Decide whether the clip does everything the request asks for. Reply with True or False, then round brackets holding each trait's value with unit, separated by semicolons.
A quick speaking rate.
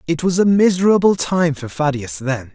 False (190 wpm)